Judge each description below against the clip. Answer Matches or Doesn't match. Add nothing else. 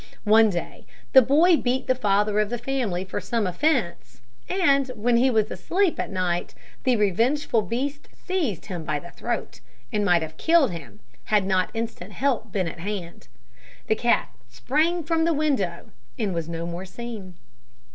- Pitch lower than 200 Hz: Doesn't match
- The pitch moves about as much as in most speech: Doesn't match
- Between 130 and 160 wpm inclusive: Doesn't match